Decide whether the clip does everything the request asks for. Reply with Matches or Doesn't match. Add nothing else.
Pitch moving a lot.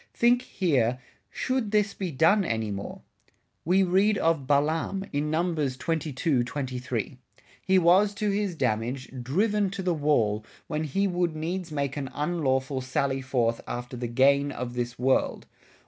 Matches